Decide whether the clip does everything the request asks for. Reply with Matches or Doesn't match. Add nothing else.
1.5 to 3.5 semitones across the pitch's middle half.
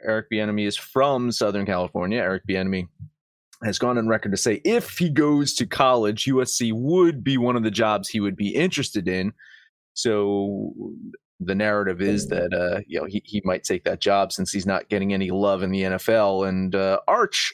Doesn't match